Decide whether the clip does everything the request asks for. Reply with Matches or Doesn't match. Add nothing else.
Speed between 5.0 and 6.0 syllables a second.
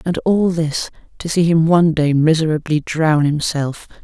Doesn't match